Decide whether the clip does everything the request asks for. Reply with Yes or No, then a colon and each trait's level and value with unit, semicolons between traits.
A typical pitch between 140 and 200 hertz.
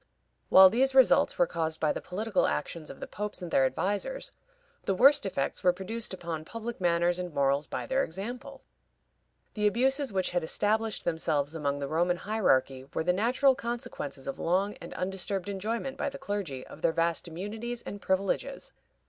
Yes: high, 190 Hz